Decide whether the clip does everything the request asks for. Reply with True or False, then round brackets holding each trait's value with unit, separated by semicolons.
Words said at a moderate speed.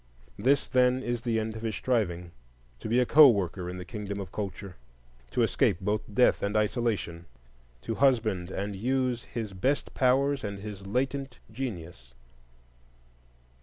True (155 wpm)